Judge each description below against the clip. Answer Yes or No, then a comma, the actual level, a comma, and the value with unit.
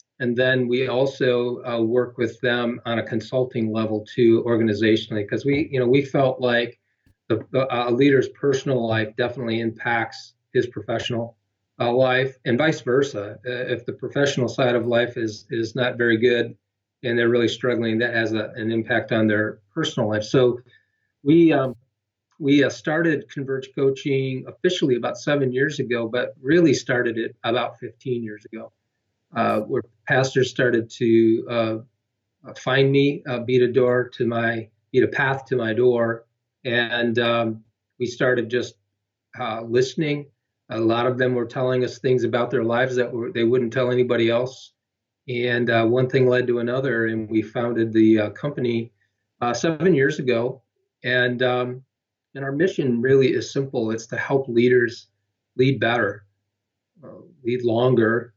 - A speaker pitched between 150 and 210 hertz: No, low, 120 Hz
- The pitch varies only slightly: Yes, narrow, 2.2 semitones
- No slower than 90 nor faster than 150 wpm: No, average, 165 wpm